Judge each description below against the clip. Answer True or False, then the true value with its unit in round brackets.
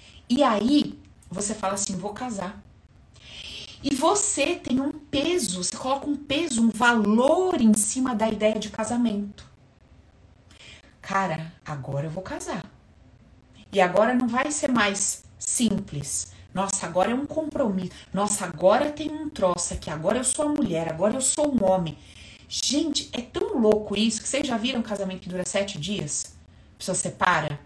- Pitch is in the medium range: False (205 Hz)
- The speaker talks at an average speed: True (160 wpm)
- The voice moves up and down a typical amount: False (6.5 semitones)